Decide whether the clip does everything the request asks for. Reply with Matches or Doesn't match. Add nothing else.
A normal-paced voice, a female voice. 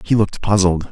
Doesn't match